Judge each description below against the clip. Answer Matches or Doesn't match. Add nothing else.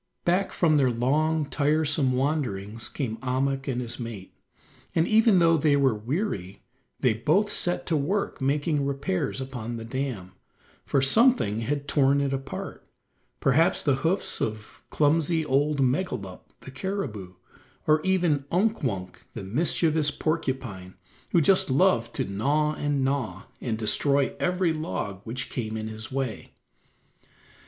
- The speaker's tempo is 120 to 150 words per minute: Matches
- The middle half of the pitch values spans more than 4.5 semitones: Matches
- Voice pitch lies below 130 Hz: Doesn't match